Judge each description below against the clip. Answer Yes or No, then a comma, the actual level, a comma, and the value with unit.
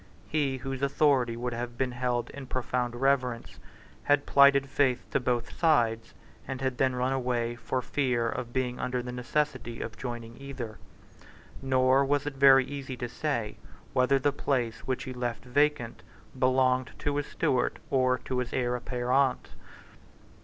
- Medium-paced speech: Yes, average, 160 wpm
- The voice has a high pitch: No, low, 130 Hz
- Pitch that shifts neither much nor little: No, narrow, 1.9 semitones